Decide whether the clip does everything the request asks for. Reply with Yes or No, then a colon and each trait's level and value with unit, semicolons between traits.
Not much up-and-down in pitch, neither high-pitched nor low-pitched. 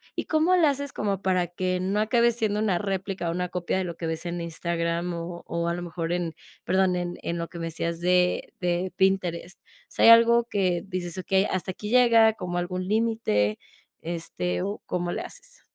No: average, 3.3 semitones; medium, 180 Hz